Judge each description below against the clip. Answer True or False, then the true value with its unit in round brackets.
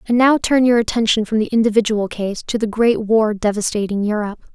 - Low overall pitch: False (220 Hz)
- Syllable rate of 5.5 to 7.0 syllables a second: True (5.8 syllables/s)